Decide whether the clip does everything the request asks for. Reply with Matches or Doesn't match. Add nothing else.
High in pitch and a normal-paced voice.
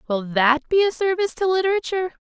Matches